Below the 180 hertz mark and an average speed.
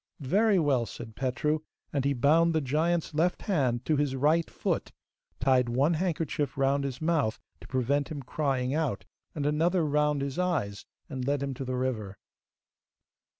Yes: medium, 140 Hz; average, 165 wpm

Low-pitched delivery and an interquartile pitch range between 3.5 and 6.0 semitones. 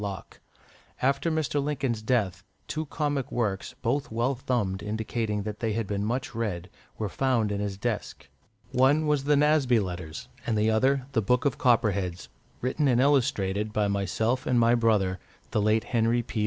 Yes: low, 115 Hz; average, 4.1 semitones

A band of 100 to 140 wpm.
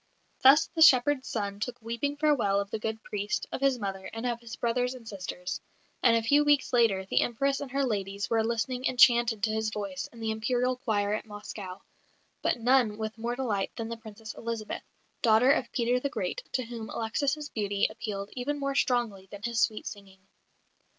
No: average, 195 wpm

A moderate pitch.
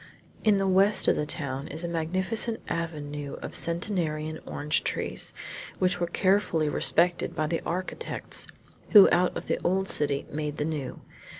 Yes: medium, 170 Hz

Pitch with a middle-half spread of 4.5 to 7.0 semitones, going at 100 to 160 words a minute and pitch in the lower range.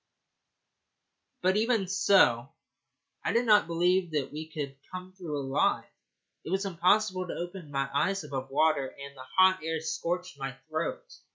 No: average, 4.9 semitones; average, 155 wpm; medium, 170 Hz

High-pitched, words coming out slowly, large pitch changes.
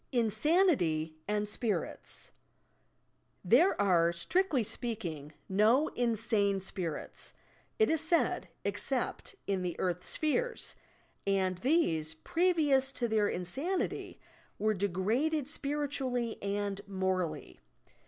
Yes: high, 215 Hz; slow, 95 wpm; wide, 7.6 semitones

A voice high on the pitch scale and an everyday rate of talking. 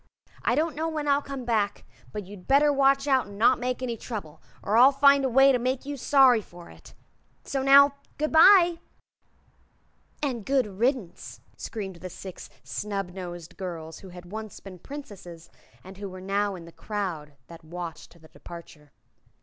Yes: high, 215 Hz; average, 175 wpm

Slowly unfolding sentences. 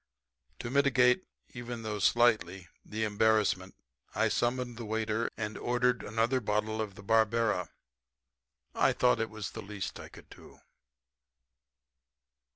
Yes: slow, 130 wpm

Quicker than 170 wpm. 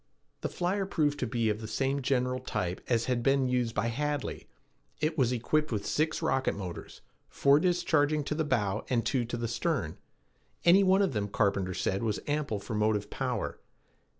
Yes: average, 185 wpm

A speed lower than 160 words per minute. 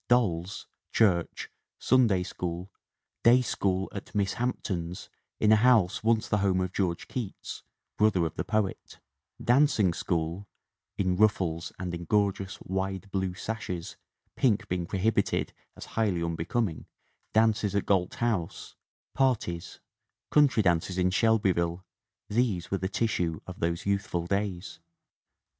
Yes: slow, 135 wpm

